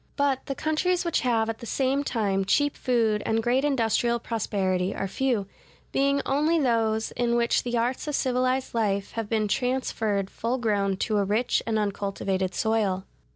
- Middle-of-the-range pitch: No, high, 230 Hz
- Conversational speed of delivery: Yes, average, 170 wpm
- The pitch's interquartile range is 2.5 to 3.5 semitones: No, average, 4.0 semitones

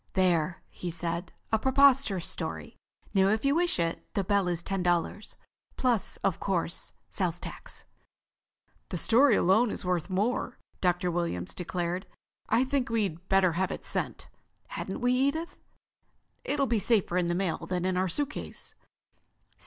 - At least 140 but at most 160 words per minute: Yes, average, 155 wpm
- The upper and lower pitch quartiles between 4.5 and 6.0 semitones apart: Yes, average, 5.1 semitones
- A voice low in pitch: No, high, 190 Hz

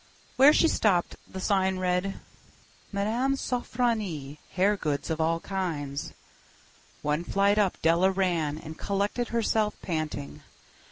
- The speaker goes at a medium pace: No, slow, 120 wpm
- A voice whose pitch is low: No, high, 190 Hz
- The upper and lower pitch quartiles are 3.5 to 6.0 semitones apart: Yes, average, 4.5 semitones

